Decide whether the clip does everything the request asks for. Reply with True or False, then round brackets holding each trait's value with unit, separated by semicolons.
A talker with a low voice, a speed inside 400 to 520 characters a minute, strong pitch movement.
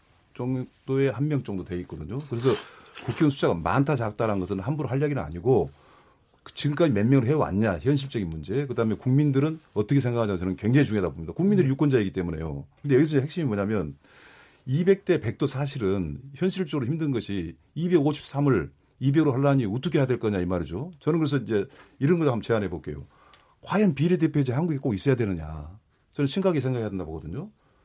True (130 Hz; 415 characters per minute; 6.7 semitones)